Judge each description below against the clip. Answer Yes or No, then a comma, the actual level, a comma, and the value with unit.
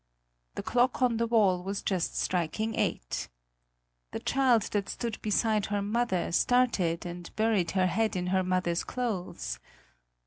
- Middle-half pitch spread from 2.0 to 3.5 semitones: No, average, 4.1 semitones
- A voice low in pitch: No, high, 200 Hz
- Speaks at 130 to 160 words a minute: Yes, average, 145 wpm